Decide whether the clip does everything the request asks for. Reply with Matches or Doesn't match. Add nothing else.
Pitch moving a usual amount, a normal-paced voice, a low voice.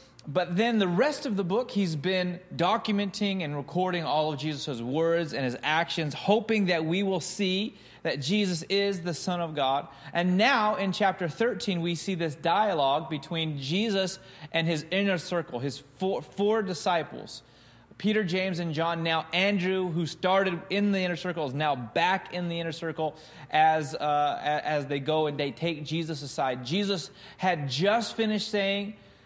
Doesn't match